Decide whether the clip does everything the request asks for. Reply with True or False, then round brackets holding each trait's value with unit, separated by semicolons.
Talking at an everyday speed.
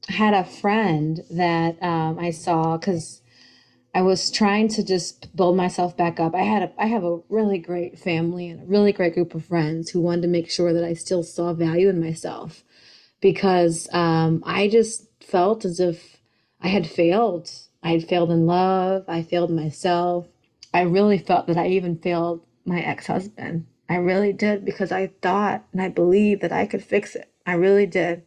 True (195 wpm)